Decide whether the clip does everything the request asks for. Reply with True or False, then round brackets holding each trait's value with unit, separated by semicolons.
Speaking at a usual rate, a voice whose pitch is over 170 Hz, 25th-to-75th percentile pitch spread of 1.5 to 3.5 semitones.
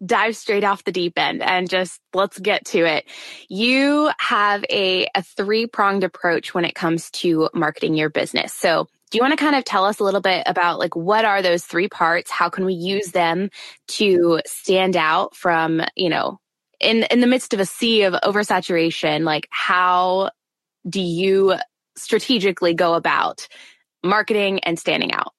True (180 wpm; 190 Hz; 3.2 semitones)